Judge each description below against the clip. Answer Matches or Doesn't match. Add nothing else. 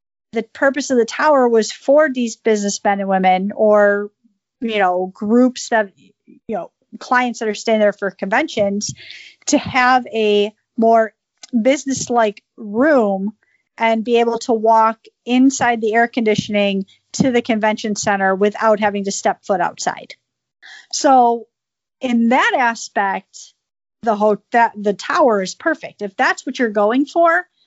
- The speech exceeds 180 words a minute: Doesn't match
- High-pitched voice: Matches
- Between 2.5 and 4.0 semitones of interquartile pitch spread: Matches